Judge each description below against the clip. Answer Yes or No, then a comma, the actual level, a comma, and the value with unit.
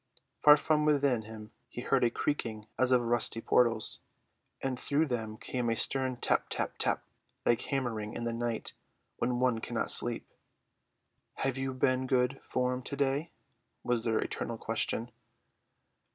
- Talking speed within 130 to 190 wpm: Yes, average, 150 wpm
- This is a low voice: Yes, low, 125 Hz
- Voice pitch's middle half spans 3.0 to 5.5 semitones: No, narrow, 2.6 semitones